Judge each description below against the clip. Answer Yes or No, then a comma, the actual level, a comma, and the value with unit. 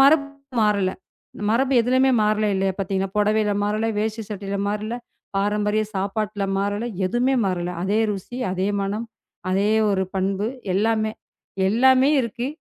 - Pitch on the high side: Yes, high, 210 Hz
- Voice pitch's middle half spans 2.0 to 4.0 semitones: Yes, narrow, 2.5 semitones